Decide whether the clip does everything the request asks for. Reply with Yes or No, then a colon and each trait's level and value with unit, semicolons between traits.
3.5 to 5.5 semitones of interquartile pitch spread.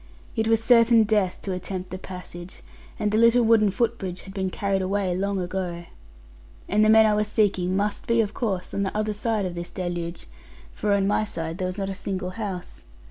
No: average, 2.7 semitones